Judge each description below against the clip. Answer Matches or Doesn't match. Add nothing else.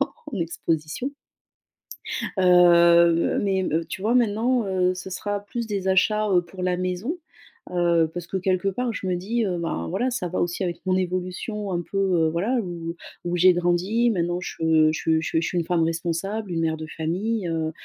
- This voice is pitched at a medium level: Matches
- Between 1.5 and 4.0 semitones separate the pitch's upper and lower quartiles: Matches